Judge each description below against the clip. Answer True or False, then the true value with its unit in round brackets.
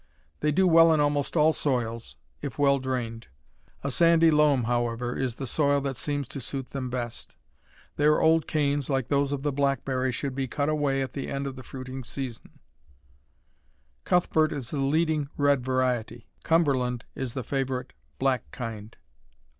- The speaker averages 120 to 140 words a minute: False (165 wpm)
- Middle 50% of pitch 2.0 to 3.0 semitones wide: True (2.5 semitones)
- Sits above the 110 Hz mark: True (135 Hz)